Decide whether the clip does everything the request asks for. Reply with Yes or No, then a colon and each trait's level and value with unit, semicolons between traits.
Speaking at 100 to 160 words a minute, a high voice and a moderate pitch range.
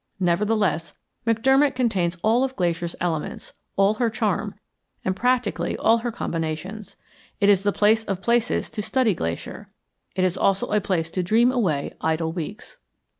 Yes: average, 155 wpm; high, 200 Hz; average, 4.9 semitones